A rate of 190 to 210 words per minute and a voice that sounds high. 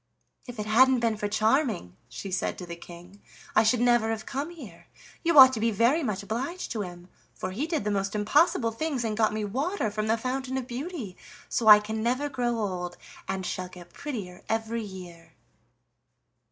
Yes: average, 195 wpm; high, 220 Hz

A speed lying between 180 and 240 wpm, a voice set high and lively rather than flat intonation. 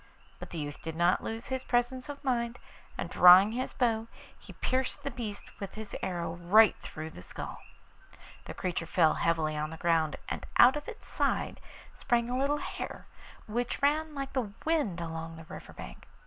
Yes: average, 185 wpm; high, 220 Hz; wide, 7.5 semitones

